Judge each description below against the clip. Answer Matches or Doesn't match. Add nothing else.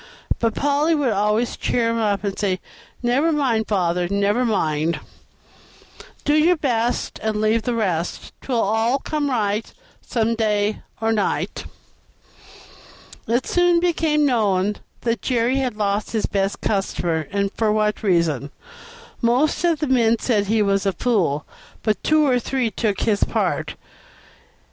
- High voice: Matches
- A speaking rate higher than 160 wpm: Doesn't match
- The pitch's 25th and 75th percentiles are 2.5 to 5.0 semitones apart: Matches